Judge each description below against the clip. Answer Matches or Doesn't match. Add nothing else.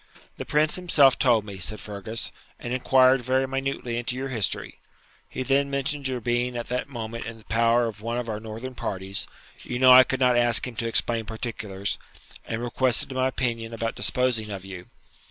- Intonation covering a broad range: Doesn't match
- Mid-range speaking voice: Doesn't match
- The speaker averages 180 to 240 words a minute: Matches